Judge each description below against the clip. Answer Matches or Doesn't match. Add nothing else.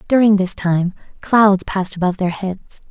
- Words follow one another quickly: Doesn't match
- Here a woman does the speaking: Matches